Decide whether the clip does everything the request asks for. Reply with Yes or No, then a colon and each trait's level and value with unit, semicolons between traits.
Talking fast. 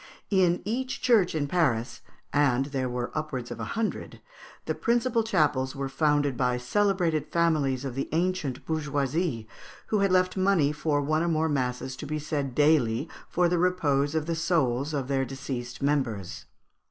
No: average, 165 wpm